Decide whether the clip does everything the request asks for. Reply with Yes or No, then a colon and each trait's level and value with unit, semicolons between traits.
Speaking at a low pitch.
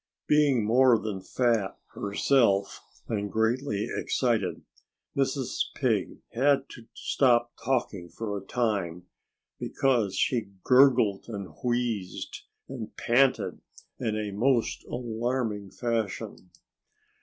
Yes: low, 115 Hz